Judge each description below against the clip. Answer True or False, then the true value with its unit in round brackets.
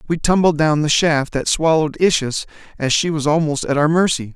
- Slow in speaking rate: False (205 wpm)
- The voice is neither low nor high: True (155 Hz)